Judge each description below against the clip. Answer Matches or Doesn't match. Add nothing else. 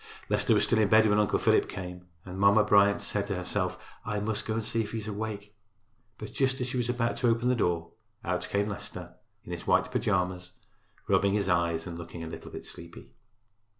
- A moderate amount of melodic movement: Matches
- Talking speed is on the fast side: Matches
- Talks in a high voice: Doesn't match